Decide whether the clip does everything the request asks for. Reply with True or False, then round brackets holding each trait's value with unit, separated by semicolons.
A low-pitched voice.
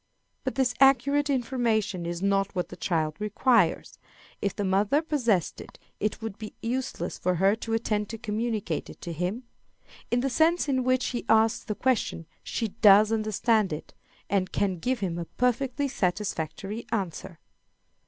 False (215 Hz)